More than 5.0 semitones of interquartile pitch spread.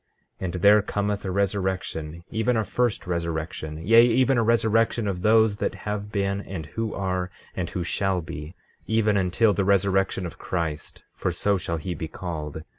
No: average, 3.6 semitones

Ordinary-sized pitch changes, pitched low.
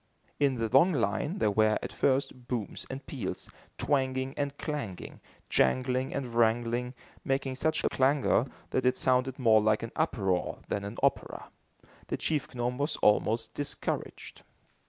Yes: average, 3.2 semitones; low, 130 Hz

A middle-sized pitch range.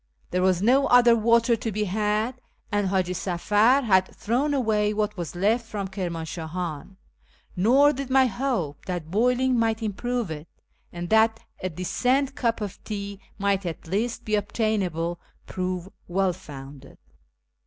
Yes: average, 4.4 semitones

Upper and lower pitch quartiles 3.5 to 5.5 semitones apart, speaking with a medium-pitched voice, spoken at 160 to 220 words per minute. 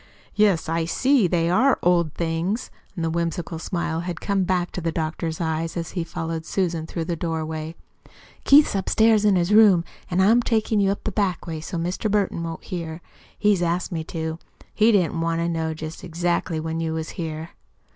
No: average, 2.8 semitones; medium, 170 Hz; average, 190 wpm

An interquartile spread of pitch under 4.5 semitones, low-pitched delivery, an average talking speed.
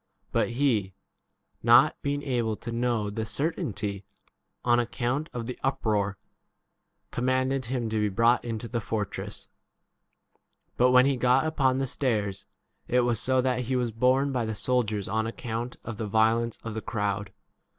Yes: average, 2.7 semitones; low, 120 Hz; average, 165 wpm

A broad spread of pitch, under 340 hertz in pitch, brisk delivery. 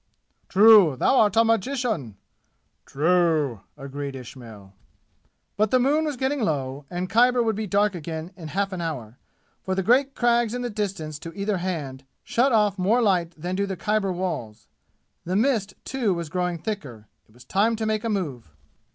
No: wide, 6.5 semitones; high, 190 Hz; average, 175 wpm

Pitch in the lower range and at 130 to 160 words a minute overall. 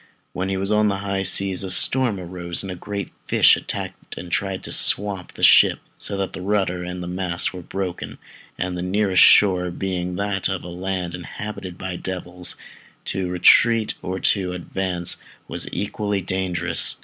No: very low, 95 Hz; average, 175 wpm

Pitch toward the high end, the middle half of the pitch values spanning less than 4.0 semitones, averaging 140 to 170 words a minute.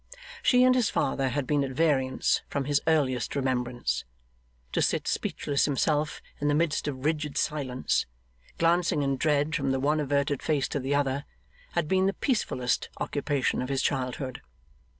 No: medium, 145 Hz; narrow, 2.4 semitones; average, 165 wpm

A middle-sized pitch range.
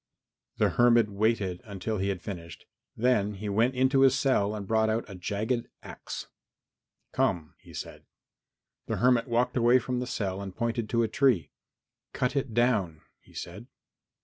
Yes: average, 3.7 semitones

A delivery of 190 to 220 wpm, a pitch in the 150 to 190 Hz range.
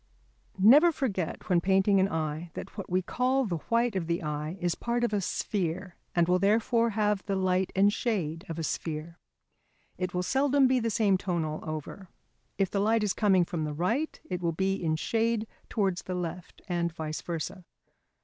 Yes: average, 195 wpm; medium, 185 Hz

